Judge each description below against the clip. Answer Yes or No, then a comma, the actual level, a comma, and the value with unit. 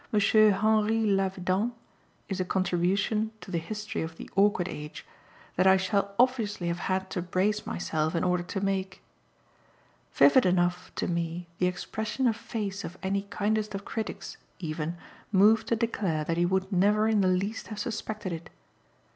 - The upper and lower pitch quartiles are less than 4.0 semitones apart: Yes, average, 3.0 semitones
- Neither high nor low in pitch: No, high, 195 Hz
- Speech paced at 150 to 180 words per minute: Yes, average, 165 wpm